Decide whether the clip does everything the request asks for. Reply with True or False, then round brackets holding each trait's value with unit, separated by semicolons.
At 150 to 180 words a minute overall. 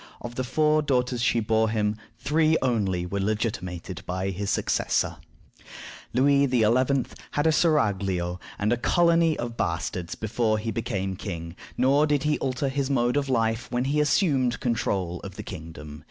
True (160 wpm)